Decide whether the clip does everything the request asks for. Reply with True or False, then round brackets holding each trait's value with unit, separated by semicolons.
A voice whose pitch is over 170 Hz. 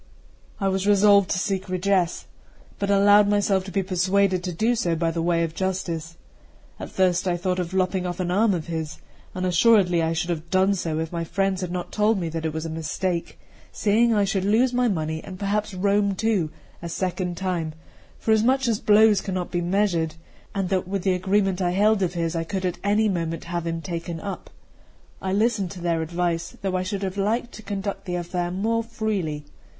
True (185 Hz)